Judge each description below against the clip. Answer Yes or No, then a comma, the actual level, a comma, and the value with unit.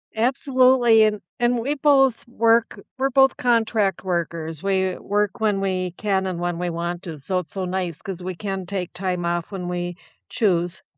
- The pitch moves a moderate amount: Yes, average, 4.3 semitones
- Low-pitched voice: No, high, 190 Hz